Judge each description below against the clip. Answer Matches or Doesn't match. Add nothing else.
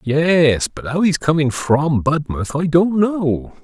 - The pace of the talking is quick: Doesn't match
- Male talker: Matches